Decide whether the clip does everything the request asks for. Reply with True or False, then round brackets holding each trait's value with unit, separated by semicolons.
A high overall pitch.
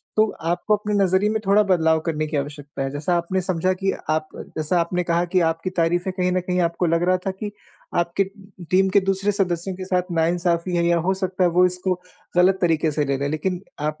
False (175 Hz)